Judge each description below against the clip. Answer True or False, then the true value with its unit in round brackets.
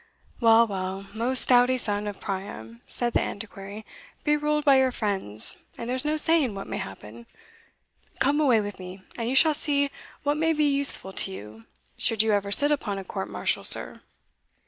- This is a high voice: True (225 Hz)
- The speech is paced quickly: False (185 wpm)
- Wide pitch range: True (6.4 semitones)